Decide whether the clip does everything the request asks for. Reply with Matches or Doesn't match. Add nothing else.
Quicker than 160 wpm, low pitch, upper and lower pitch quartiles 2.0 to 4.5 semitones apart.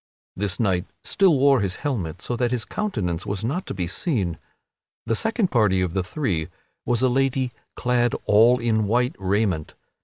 Doesn't match